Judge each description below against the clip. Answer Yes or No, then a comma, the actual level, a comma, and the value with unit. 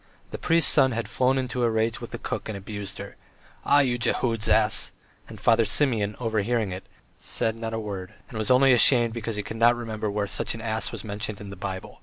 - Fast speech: Yes, fast, 225 wpm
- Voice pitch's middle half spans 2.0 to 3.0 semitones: Yes, narrow, 2.4 semitones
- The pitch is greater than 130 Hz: No, low, 110 Hz